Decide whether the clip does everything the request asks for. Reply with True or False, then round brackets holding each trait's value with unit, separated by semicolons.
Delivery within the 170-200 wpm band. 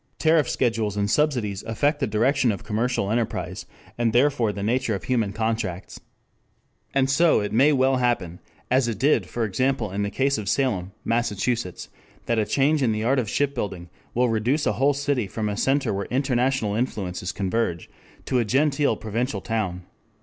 True (175 wpm)